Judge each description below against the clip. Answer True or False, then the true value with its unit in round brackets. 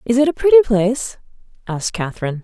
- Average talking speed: True (175 wpm)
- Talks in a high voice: True (230 Hz)